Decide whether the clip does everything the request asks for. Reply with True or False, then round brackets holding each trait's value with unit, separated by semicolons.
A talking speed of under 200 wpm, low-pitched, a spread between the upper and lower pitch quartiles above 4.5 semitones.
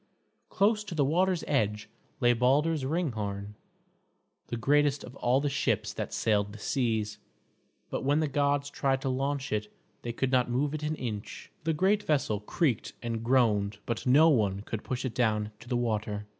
True (180 wpm; 130 Hz; 5.0 semitones)